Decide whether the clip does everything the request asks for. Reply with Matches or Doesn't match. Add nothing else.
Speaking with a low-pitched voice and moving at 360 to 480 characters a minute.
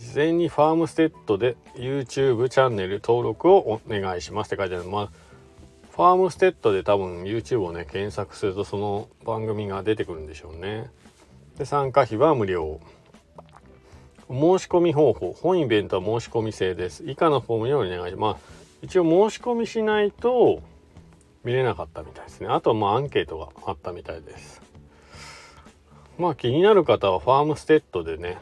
Matches